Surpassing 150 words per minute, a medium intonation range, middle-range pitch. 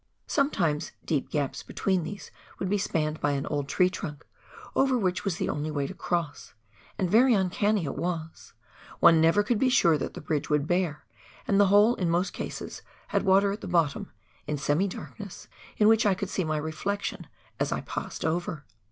Yes: average, 195 wpm; average, 4.7 semitones; medium, 175 Hz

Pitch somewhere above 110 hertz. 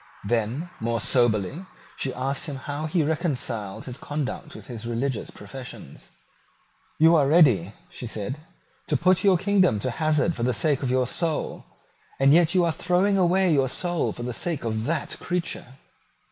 Yes: medium, 140 Hz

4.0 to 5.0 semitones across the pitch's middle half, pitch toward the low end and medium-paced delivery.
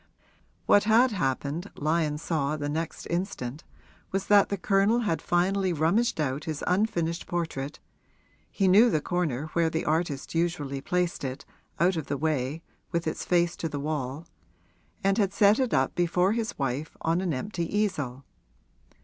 No: average, 4.6 semitones; medium, 170 Hz; average, 160 wpm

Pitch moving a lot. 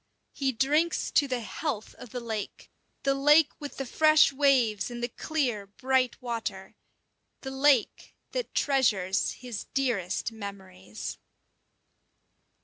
No: average, 4.7 semitones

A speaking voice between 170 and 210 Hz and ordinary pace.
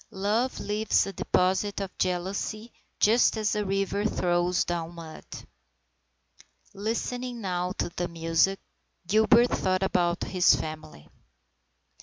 No: high, 190 Hz; slow, 115 wpm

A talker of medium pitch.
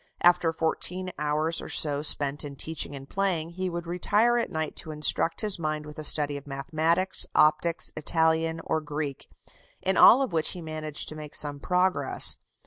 Yes: medium, 160 Hz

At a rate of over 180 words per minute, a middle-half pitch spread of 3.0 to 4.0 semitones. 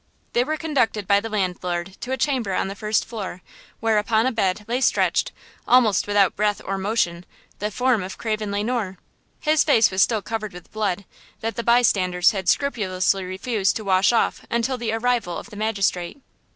Yes: average, 190 wpm; average, 3.5 semitones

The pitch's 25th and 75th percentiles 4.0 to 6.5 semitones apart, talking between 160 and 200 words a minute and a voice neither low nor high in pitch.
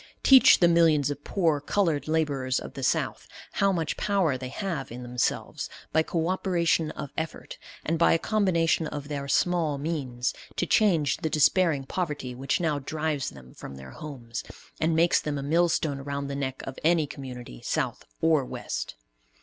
No: average, 3.5 semitones; average, 175 wpm; medium, 150 Hz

